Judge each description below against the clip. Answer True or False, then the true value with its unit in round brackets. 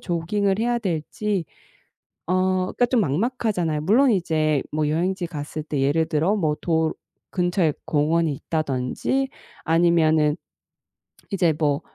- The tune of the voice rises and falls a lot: False (3.8 semitones)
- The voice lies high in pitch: False (165 Hz)